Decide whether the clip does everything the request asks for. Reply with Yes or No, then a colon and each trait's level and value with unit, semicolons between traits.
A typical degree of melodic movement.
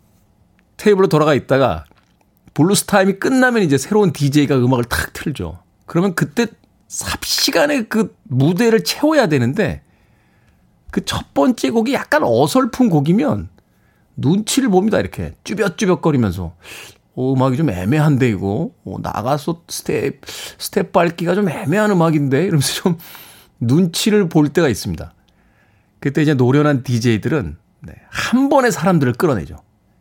No: wide, 8.6 semitones